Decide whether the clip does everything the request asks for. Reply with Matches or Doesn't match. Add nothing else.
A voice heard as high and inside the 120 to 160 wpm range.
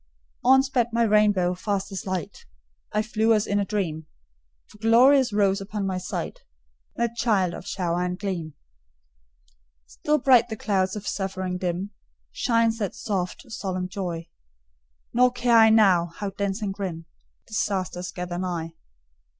Matches